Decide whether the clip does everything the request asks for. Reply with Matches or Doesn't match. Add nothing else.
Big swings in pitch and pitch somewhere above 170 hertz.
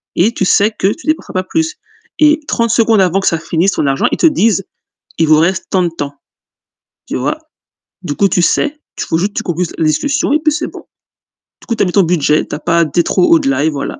Matches